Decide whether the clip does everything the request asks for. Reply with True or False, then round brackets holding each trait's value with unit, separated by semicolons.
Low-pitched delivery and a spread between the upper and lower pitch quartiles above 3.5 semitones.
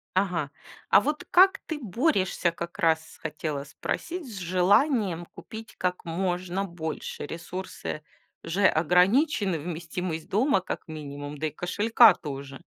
False (180 Hz; 4.2 semitones)